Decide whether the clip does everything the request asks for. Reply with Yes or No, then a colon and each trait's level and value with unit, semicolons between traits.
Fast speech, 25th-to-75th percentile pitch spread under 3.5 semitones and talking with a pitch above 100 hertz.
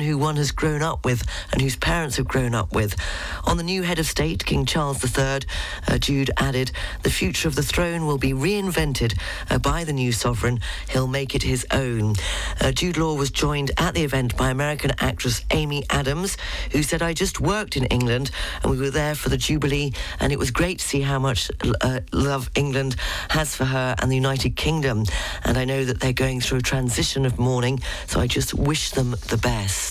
Yes: fast, 215 wpm; average, 2.9 semitones; low, 135 Hz